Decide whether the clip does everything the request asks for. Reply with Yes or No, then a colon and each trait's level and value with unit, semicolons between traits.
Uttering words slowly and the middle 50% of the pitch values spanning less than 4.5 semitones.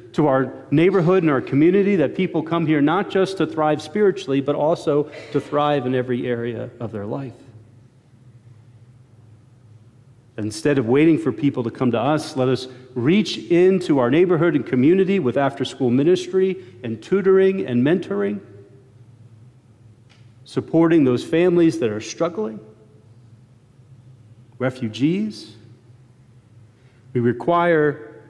No: slow, 125 wpm; average, 5.2 semitones